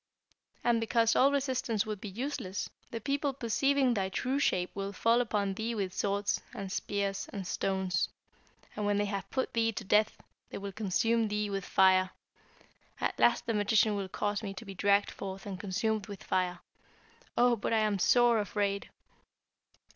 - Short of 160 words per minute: No, average, 175 wpm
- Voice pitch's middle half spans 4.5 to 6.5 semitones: No, average, 2.7 semitones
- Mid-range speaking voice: No, high, 205 Hz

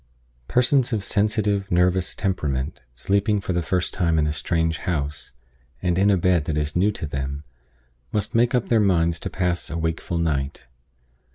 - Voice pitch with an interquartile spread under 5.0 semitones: Yes, average, 4.2 semitones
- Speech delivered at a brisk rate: No, average, 175 wpm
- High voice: No, very low, 90 Hz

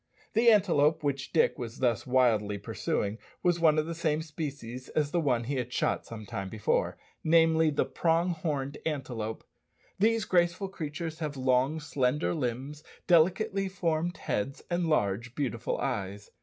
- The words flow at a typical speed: Yes, average, 150 wpm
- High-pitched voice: No, medium, 150 Hz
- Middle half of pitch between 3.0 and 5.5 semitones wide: Yes, average, 5.0 semitones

